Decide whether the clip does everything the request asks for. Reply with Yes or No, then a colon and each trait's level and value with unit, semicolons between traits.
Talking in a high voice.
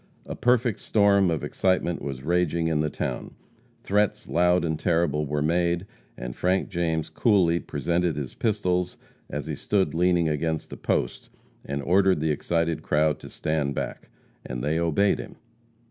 No: very low, 85 Hz